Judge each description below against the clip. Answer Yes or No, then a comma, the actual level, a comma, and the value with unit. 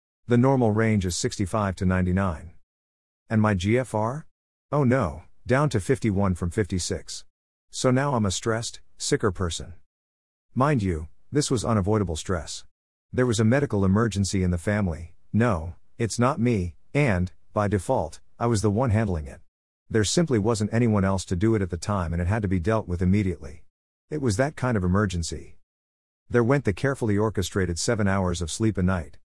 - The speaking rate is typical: Yes, average, 180 wpm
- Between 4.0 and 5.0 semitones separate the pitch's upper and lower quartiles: Yes, average, 4.6 semitones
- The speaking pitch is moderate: No, low, 100 Hz